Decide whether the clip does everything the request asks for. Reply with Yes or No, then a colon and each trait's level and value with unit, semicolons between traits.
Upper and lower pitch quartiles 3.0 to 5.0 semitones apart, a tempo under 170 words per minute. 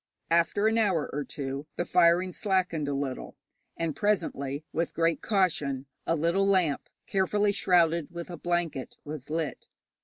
Yes: average, 3.9 semitones; average, 150 wpm